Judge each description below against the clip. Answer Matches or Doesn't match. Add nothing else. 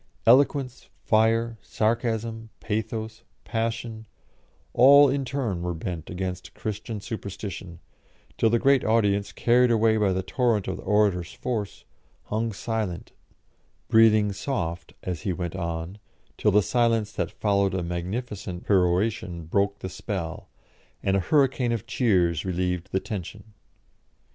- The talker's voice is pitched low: Matches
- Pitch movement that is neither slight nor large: Matches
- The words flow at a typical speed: Doesn't match